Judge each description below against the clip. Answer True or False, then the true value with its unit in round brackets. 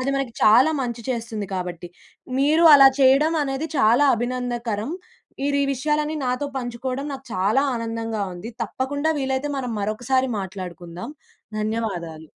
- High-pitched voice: True (245 Hz)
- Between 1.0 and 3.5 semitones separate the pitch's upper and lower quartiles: False (4.1 semitones)